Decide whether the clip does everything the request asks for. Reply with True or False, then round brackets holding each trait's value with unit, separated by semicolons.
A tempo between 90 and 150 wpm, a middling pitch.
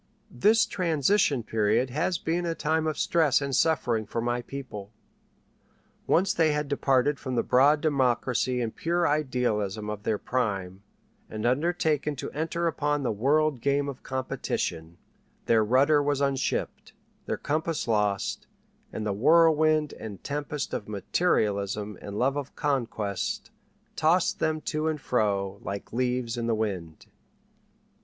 False (140 wpm; 130 Hz)